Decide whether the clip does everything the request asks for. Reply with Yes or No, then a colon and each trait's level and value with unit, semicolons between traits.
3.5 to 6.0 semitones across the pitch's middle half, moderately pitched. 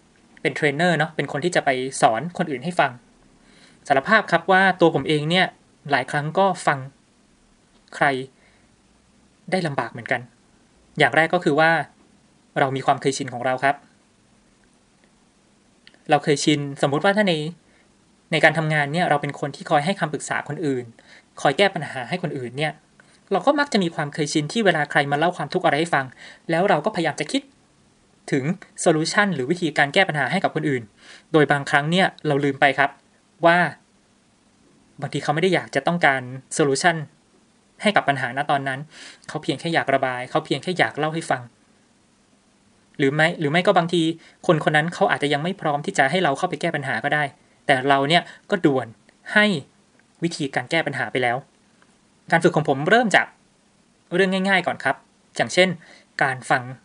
Yes: average, 4.2 semitones; medium, 155 Hz